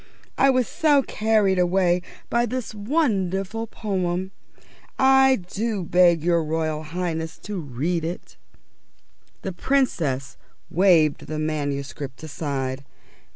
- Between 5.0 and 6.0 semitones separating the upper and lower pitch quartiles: Yes, wide, 5.6 semitones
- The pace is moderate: No, slow, 110 wpm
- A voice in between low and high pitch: Yes, medium, 180 Hz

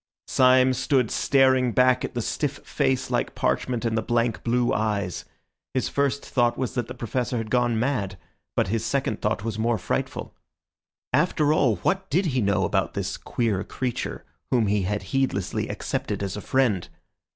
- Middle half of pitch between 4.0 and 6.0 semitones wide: No, average, 3.3 semitones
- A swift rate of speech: No, average, 175 wpm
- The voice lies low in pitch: Yes, low, 120 Hz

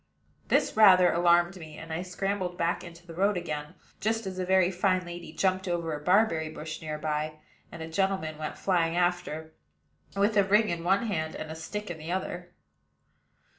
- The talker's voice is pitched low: No, medium, 175 Hz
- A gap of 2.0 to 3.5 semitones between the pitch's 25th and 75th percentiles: Yes, average, 2.9 semitones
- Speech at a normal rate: Yes, average, 190 wpm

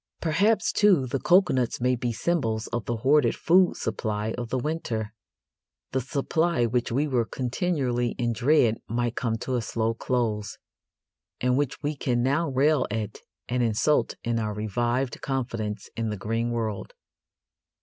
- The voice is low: Yes, low, 120 Hz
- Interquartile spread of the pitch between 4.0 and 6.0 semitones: No, average, 3.6 semitones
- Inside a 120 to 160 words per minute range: Yes, average, 155 wpm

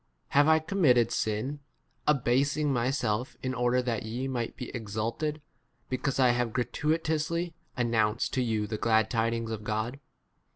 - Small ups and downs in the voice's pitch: No, average, 4.0 semitones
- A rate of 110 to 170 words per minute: Yes, average, 155 wpm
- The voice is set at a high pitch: No, low, 125 Hz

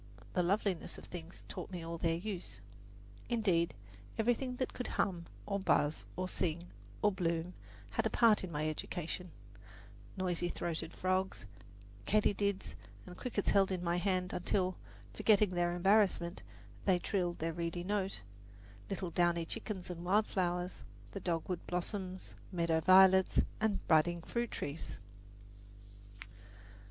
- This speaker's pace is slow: Yes, slow, 130 wpm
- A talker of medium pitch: Yes, medium, 180 Hz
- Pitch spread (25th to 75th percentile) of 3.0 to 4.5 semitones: No, narrow, 2.5 semitones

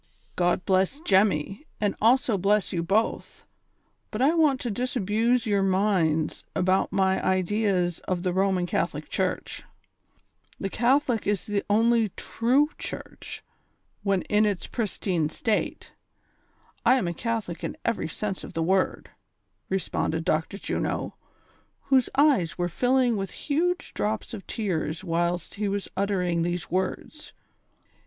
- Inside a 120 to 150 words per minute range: Yes, slow, 135 wpm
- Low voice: No, high, 200 Hz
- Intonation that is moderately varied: Yes, average, 4.2 semitones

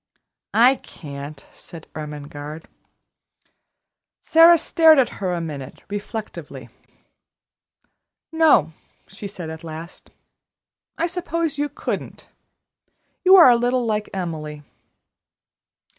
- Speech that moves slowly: Yes, slow, 100 wpm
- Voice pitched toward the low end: No, high, 195 Hz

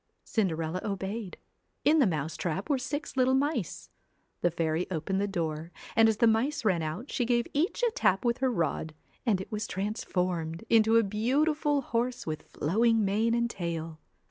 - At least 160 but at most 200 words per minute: Yes, average, 180 wpm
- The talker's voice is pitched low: No, high, 210 Hz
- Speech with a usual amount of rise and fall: No, wide, 6.0 semitones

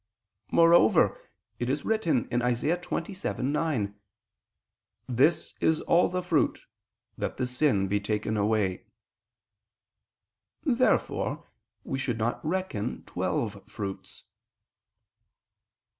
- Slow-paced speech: Yes, slow, 90 wpm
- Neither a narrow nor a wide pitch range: No, wide, 7.5 semitones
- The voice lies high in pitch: No, low, 125 Hz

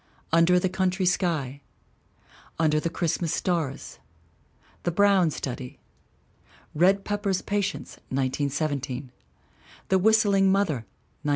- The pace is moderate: No, slow, 100 wpm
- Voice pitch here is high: No, medium, 170 Hz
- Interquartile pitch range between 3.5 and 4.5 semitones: No, average, 5.1 semitones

